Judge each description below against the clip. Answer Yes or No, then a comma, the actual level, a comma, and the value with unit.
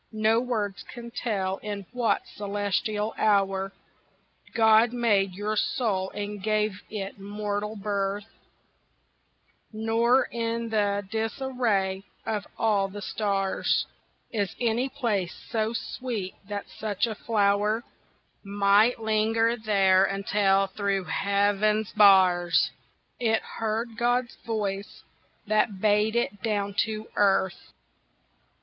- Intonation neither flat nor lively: No, narrow, 2.1 semitones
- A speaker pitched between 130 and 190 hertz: No, high, 210 Hz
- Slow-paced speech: Yes, slow, 105 wpm